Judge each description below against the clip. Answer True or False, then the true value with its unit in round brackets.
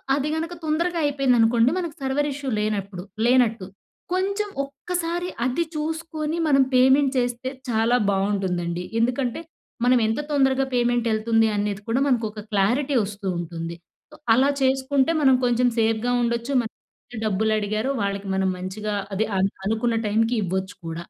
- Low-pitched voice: False (240 Hz)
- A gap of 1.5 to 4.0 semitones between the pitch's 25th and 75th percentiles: False (4.8 semitones)